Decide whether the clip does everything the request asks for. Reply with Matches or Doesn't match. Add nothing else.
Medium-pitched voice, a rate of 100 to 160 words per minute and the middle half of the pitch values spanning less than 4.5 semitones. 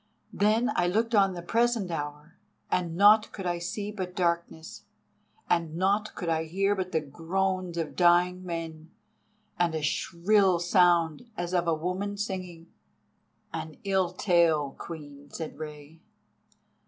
Matches